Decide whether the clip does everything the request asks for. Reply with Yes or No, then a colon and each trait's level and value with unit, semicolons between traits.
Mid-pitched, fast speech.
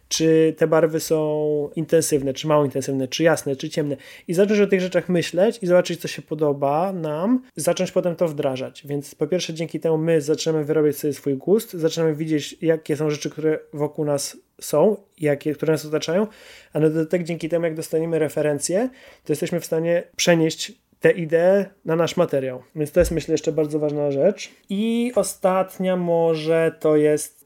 Yes: medium, 160 Hz; fast, 180 wpm